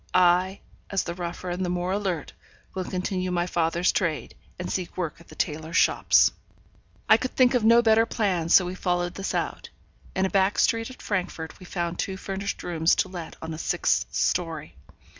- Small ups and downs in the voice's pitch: Yes, narrow, 2.1 semitones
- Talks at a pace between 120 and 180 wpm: No, average, 195 wpm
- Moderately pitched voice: Yes, medium, 180 Hz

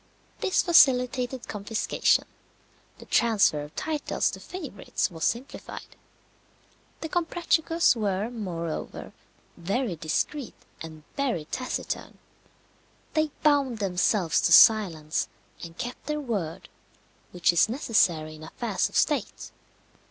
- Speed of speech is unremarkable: No, slow, 105 wpm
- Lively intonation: Yes, wide, 8.0 semitones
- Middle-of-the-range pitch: No, high, 220 Hz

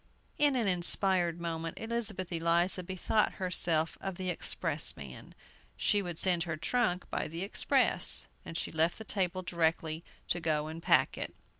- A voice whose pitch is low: No, medium, 175 Hz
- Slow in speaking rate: No, average, 155 wpm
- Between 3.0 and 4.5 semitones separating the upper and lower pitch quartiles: No, narrow, 2.6 semitones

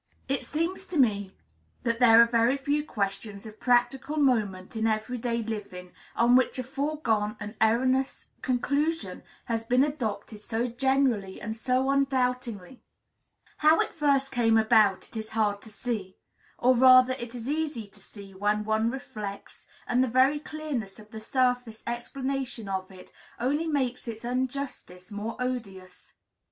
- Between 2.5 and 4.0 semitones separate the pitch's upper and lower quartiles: Yes, average, 3.6 semitones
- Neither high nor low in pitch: No, high, 240 Hz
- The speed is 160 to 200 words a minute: No, average, 150 wpm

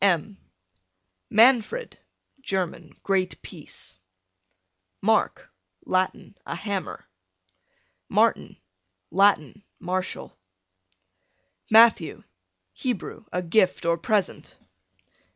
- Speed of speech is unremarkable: No, slow, 70 wpm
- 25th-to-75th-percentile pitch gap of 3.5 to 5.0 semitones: No, average, 3.1 semitones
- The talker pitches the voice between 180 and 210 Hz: Yes, high, 190 Hz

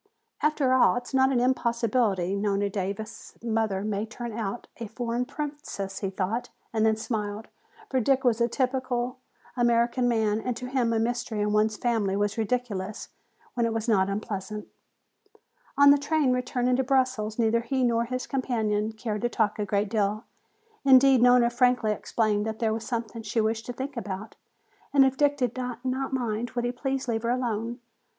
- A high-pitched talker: Yes, high, 235 Hz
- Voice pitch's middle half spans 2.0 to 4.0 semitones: Yes, average, 2.8 semitones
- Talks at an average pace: Yes, average, 180 wpm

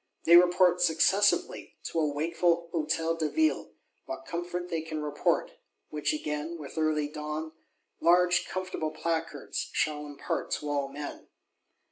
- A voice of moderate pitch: Yes, medium, 160 Hz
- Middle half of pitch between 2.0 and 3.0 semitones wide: Yes, narrow, 2.4 semitones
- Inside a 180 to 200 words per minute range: No, slow, 135 wpm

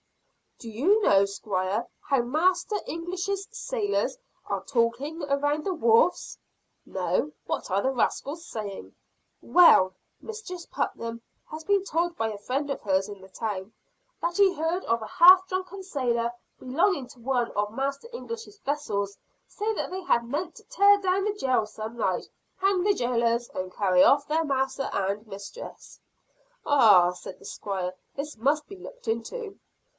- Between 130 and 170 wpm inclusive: Yes, average, 155 wpm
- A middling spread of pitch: No, wide, 8.7 semitones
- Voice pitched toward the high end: Yes, very high, 275 Hz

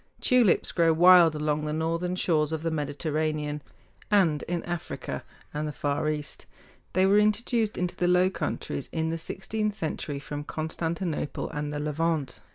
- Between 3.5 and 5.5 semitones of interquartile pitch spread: No, average, 3.1 semitones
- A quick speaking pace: No, average, 160 wpm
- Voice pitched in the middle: Yes, medium, 160 Hz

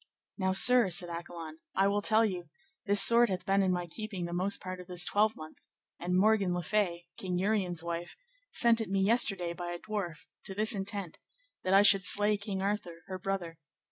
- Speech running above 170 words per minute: Yes, average, 200 wpm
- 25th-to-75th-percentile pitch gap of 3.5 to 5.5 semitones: No, average, 2.9 semitones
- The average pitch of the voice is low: No, high, 190 Hz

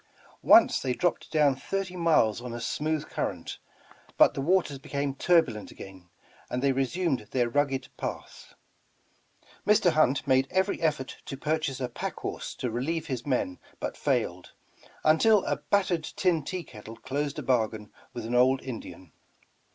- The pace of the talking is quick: No, average, 160 wpm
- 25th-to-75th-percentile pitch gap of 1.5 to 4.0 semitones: No, average, 4.8 semitones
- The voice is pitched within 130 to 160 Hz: Yes, low, 135 Hz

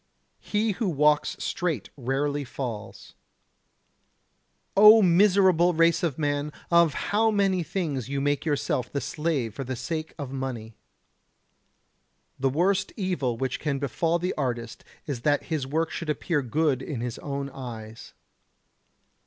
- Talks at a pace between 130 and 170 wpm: Yes, slow, 135 wpm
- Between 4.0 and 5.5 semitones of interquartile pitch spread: Yes, average, 4.5 semitones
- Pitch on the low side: No, medium, 145 Hz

